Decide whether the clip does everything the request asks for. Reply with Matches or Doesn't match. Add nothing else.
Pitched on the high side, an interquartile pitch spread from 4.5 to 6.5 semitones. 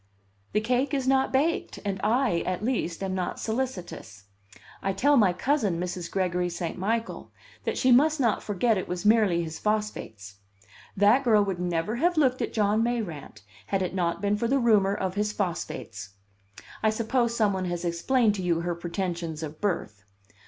Matches